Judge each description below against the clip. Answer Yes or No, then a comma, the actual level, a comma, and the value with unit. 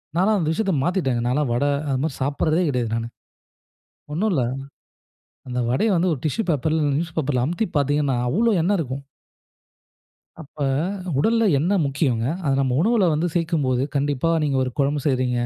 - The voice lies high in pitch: No, medium, 145 Hz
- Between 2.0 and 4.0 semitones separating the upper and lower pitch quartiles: No, average, 4.7 semitones